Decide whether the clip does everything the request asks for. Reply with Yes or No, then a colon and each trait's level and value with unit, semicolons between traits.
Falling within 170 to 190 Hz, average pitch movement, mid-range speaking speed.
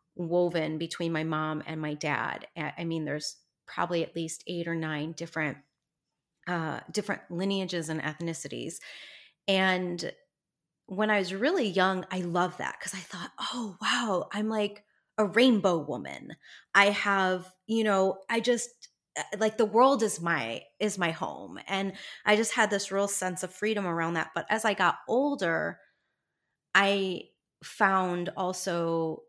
Yes: medium, 185 Hz; average, 3.9 semitones; average, 150 wpm